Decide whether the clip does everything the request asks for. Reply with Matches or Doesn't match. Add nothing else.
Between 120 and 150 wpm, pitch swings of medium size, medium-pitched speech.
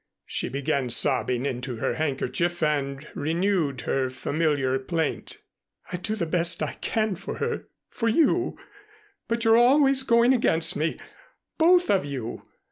Doesn't match